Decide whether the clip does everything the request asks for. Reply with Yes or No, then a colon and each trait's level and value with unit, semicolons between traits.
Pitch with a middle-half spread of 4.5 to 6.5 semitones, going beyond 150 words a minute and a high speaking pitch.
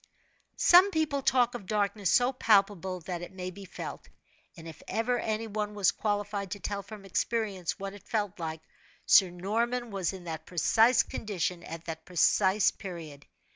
No: average, 3.6 semitones; average, 170 wpm; high, 200 Hz